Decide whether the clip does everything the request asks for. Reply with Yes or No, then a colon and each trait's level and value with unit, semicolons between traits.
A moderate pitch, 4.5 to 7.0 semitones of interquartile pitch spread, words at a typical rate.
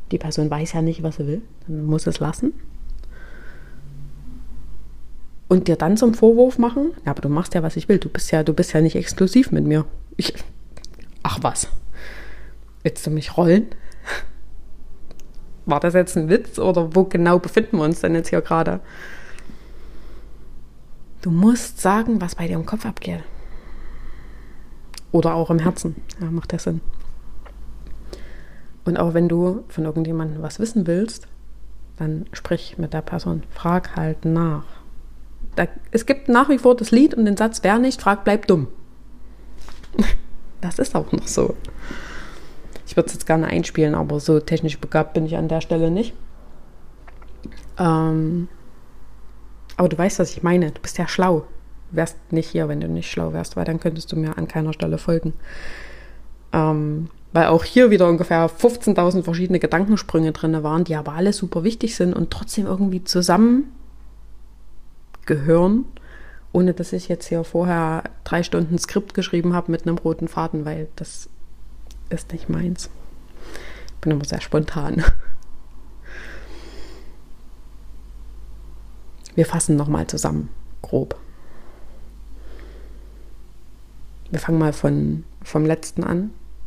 No: medium, 165 Hz; average, 2.7 semitones; average, 150 wpm